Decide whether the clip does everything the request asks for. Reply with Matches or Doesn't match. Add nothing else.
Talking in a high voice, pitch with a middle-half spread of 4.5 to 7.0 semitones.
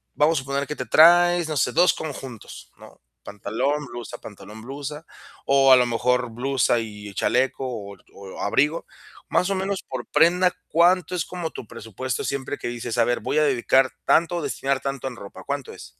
Doesn't match